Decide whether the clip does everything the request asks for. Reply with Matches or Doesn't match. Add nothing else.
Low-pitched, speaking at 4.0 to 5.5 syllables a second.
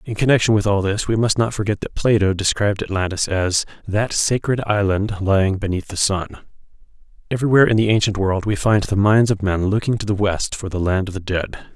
Doesn't match